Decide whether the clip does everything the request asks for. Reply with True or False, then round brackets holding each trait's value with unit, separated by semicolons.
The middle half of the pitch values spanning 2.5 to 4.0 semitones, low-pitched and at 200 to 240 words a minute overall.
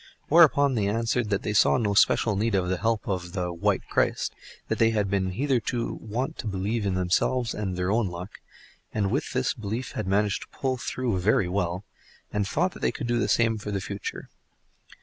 True (3.6 semitones; 105 Hz; 205 wpm)